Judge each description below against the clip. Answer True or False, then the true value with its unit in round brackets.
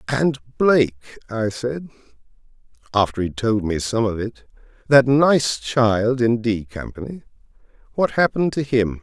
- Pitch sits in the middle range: False (120 Hz)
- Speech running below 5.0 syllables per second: True (4.4 syllables/s)